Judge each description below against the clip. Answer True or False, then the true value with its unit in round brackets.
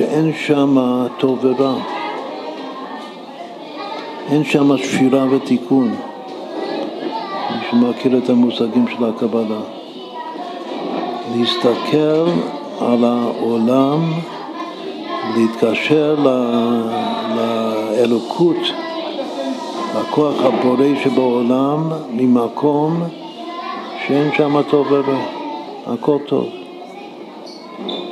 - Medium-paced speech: False (60 wpm)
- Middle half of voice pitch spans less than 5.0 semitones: True (4.1 semitones)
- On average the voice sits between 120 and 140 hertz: True (135 Hz)